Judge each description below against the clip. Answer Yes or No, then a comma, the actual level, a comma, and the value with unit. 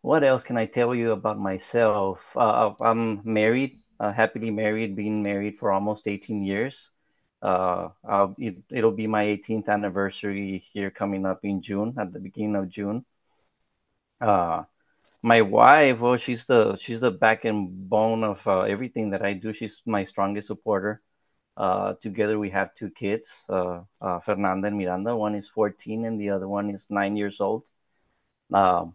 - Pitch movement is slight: Yes, narrow, 2.1 semitones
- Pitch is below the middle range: Yes, low, 105 Hz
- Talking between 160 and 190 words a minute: Yes, average, 170 wpm